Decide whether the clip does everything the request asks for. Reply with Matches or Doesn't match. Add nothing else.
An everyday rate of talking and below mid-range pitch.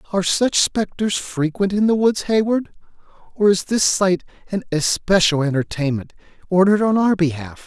Doesn't match